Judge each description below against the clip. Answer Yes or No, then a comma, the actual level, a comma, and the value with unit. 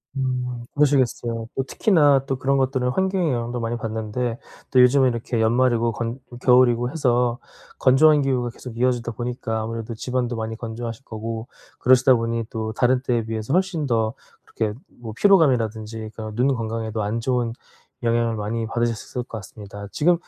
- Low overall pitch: Yes, low, 120 Hz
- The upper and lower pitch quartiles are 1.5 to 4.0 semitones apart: Yes, narrow, 2.4 semitones